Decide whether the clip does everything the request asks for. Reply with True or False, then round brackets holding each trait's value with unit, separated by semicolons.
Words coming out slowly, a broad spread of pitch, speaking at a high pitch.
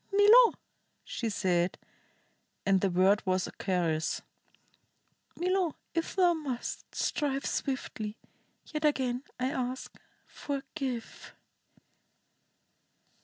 True (90 wpm; 7.8 semitones; 255 Hz)